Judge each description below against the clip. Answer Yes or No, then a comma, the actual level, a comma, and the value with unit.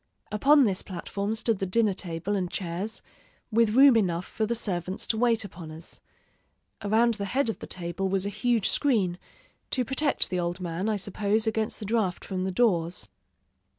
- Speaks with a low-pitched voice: No, high, 200 Hz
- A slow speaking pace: No, average, 185 wpm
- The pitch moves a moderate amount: Yes, average, 3.7 semitones